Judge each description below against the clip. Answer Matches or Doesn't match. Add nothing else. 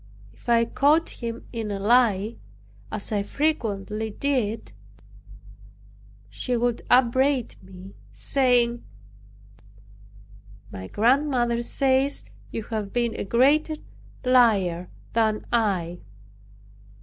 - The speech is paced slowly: Matches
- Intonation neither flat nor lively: Matches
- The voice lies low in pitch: Doesn't match